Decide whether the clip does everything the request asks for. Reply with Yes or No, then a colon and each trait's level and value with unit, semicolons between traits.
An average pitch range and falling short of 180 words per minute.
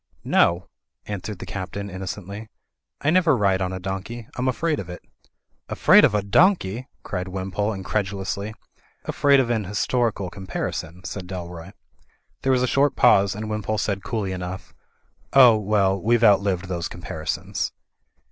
Yes: average, 3.5 semitones; average, 150 wpm